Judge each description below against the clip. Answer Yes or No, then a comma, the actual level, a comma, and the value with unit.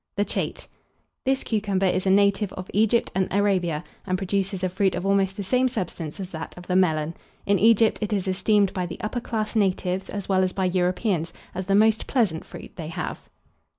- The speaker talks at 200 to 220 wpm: Yes, fast, 205 wpm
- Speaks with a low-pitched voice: No, high, 195 Hz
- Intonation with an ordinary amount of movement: No, narrow, 2.3 semitones